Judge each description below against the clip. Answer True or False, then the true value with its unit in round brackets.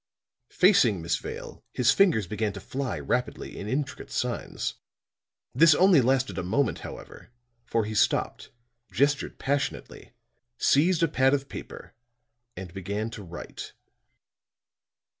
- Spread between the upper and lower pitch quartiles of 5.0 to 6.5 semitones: True (5.5 semitones)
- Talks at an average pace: False (125 wpm)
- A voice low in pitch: True (125 Hz)